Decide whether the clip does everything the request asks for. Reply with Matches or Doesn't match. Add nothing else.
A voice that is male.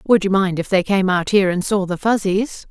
Doesn't match